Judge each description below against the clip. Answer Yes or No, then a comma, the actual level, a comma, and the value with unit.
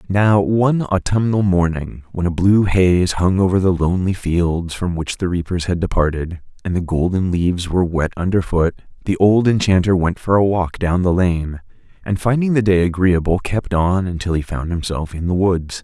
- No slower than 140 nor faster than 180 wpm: No, average, 190 wpm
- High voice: No, very low, 90 Hz